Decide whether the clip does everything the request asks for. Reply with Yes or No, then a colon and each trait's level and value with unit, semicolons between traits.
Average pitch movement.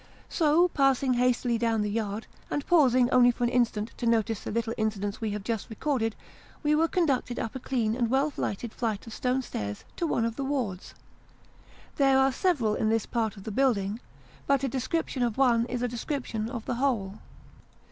Yes: average, 3.4 semitones